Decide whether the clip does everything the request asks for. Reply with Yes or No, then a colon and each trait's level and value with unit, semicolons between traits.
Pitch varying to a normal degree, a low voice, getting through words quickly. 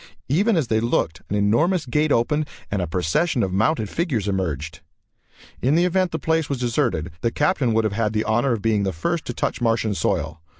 No: wide, 7.3 semitones; low, 115 Hz; fast, 210 wpm